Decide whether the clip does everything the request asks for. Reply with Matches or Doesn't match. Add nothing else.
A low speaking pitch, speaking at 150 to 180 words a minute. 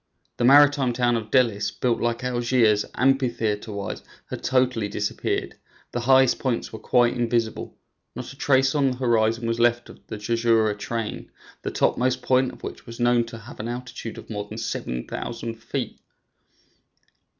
Matches